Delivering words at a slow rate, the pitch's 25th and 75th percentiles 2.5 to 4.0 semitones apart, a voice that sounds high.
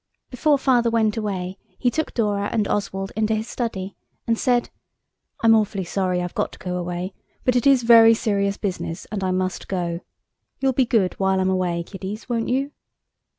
No: average, 185 wpm; average, 3.7 semitones; high, 205 Hz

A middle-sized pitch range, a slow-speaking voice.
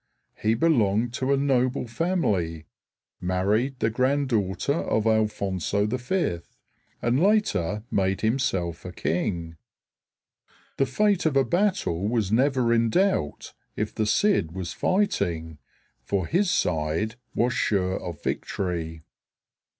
No: wide, 6.7 semitones; slow, 120 wpm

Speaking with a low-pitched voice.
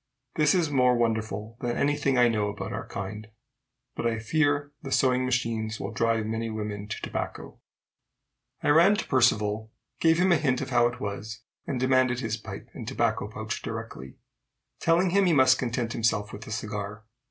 Yes: low, 120 Hz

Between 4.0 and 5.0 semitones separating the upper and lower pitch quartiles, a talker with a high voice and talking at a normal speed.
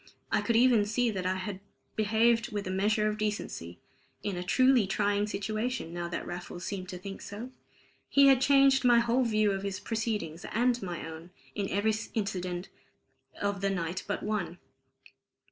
No: average, 3.6 semitones; high, 205 Hz; average, 175 wpm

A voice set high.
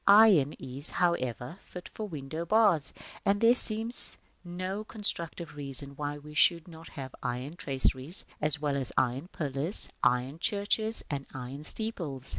No: medium, 155 Hz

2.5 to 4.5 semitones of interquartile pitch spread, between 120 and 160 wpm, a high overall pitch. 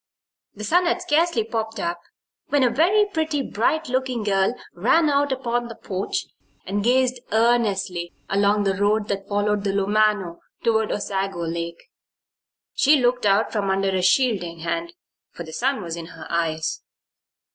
No: average, 4.9 semitones; average, 155 wpm; high, 210 Hz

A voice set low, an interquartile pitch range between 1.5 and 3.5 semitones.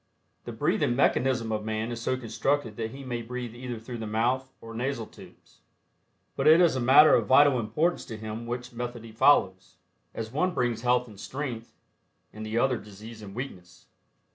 Yes: low, 120 Hz; average, 2.7 semitones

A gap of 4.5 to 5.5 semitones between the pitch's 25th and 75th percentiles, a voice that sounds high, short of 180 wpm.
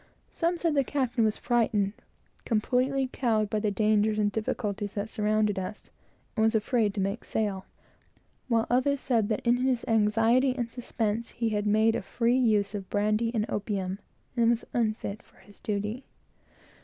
No: narrow, 2.5 semitones; high, 220 Hz; average, 170 wpm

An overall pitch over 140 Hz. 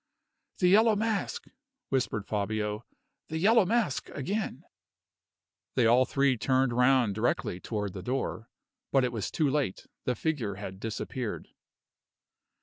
No: low, 125 Hz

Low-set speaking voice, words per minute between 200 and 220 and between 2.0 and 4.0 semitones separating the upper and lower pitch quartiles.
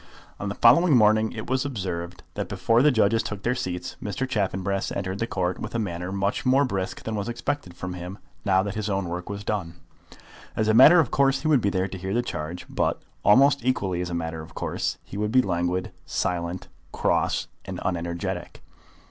No: low, 100 Hz; fast, 205 wpm; average, 4.7 semitones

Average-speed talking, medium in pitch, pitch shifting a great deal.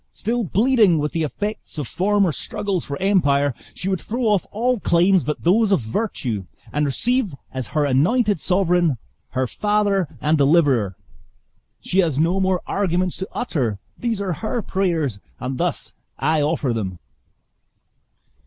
Yes: average, 150 wpm; medium, 175 Hz; wide, 6.0 semitones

